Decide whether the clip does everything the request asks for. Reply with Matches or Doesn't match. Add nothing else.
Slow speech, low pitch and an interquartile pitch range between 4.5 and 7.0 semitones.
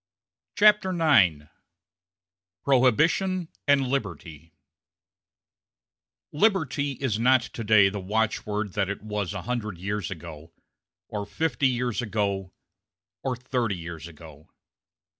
Matches